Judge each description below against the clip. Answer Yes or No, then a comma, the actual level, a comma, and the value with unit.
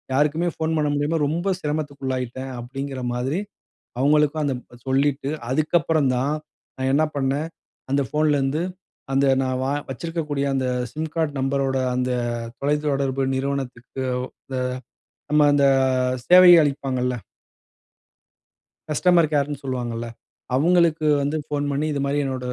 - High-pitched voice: No, medium, 140 Hz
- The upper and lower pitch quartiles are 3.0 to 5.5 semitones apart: No, narrow, 2.4 semitones